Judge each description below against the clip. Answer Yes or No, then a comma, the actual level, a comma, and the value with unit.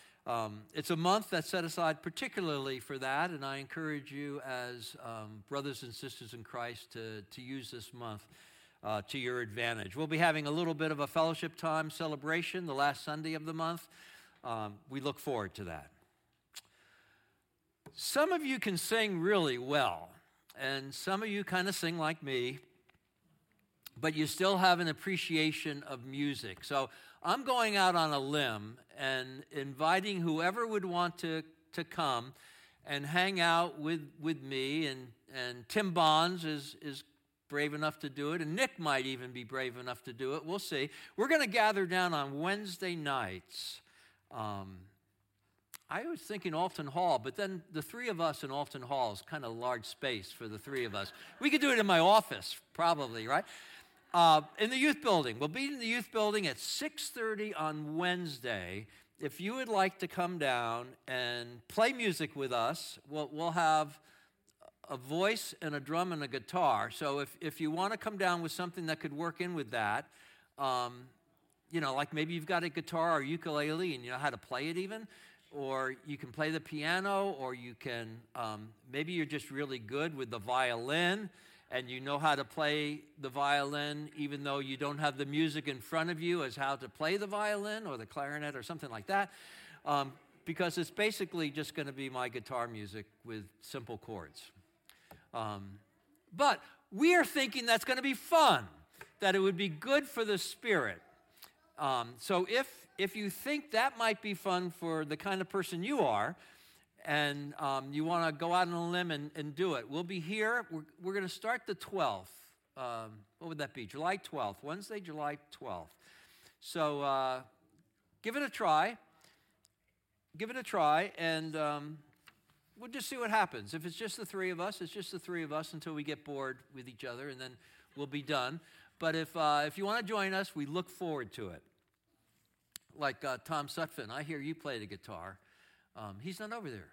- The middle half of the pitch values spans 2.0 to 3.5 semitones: No, average, 5.2 semitones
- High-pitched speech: No, medium, 155 Hz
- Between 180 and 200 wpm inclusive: Yes, average, 195 wpm